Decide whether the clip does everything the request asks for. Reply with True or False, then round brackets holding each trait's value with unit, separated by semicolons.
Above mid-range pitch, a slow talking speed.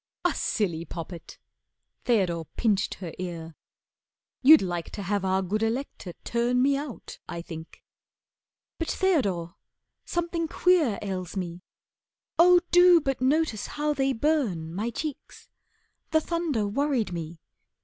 True (225 Hz; 130 wpm)